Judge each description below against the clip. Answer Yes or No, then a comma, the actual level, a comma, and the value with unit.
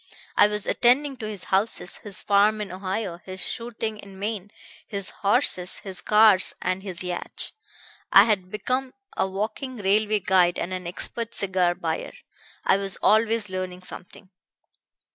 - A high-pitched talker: Yes, high, 200 Hz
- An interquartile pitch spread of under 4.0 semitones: Yes, average, 2.7 semitones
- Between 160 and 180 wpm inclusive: No, average, 150 wpm